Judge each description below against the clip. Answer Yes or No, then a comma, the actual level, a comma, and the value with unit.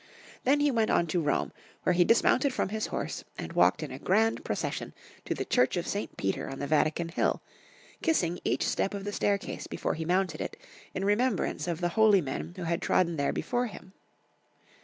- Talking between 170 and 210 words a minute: Yes, average, 200 wpm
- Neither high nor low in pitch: Yes, medium, 180 Hz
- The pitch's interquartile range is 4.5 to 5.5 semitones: Yes, average, 4.9 semitones